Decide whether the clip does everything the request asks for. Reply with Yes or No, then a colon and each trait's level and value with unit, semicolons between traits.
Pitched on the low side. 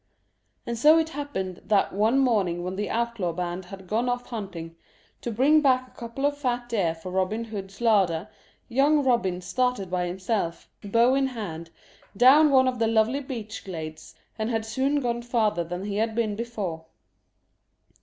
No: high, 225 Hz